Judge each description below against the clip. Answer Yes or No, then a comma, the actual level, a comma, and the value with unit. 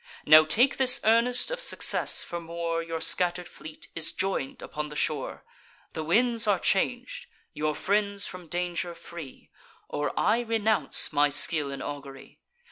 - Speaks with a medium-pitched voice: Yes, medium, 170 Hz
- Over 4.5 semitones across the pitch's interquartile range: Yes, wide, 5.6 semitones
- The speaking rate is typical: Yes, average, 150 wpm